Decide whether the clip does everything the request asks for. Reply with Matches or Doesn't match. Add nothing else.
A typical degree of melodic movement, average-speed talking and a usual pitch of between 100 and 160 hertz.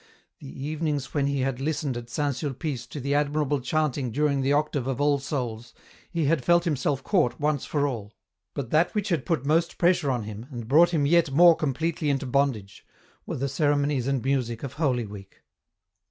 Doesn't match